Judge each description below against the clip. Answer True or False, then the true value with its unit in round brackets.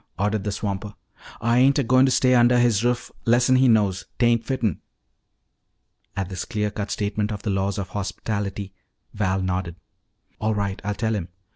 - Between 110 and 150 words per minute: False (175 wpm)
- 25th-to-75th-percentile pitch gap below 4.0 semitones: True (3.1 semitones)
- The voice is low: True (105 Hz)